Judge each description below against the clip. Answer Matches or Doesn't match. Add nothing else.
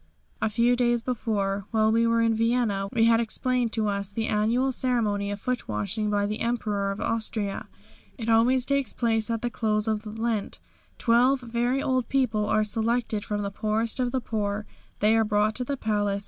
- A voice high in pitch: Matches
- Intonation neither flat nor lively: Doesn't match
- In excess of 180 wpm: Matches